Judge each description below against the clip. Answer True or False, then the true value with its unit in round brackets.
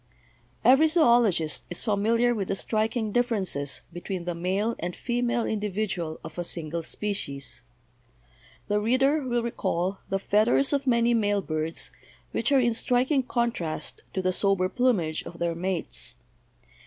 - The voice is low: False (210 Hz)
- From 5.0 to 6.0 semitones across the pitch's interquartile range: True (5.4 semitones)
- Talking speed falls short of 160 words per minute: True (145 wpm)